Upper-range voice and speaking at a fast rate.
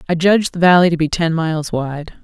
No: medium, 165 Hz; fast, 240 wpm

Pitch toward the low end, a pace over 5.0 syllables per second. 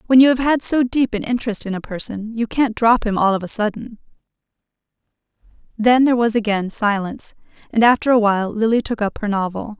No: high, 220 Hz; 5.9 syllables/s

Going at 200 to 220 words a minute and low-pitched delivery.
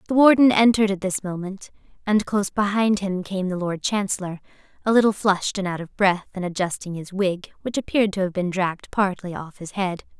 No: fast, 205 wpm; high, 195 Hz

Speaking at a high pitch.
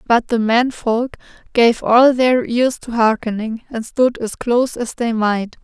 Yes: high, 235 Hz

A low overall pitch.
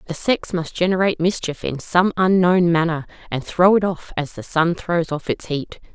No: medium, 170 Hz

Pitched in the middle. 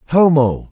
Yes: medium, 150 Hz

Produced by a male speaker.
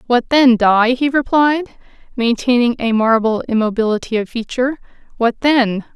No: female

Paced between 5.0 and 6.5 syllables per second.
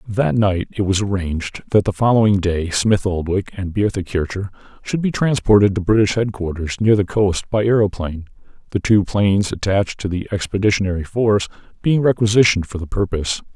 Yes: 5.7 syllables/s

